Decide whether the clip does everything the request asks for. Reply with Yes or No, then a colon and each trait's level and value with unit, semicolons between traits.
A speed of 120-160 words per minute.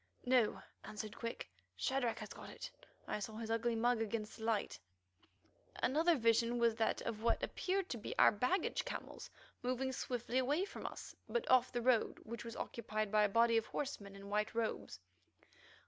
No: average, 180 wpm